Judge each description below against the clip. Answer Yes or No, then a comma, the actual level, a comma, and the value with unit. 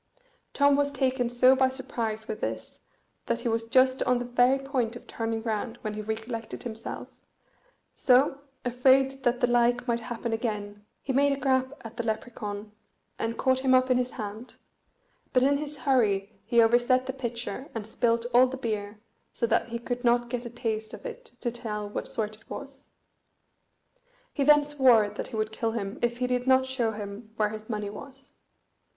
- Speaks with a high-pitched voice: Yes, high, 240 Hz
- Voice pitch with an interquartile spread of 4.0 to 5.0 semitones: No, average, 2.8 semitones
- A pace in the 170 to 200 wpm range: Yes, average, 190 wpm